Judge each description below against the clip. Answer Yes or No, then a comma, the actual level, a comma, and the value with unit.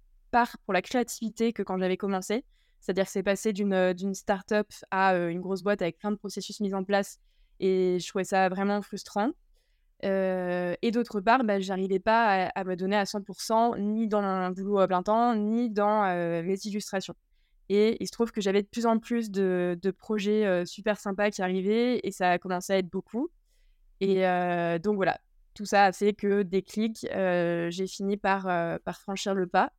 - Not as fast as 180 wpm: No, average, 205 wpm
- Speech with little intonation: Yes, narrow, 2.1 semitones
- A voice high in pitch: Yes, high, 200 Hz